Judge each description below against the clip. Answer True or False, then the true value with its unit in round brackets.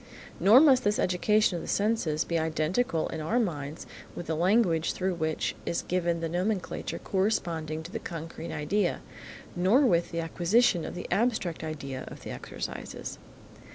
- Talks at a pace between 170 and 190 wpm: False (160 wpm)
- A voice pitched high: False (175 Hz)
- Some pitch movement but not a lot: True (4.4 semitones)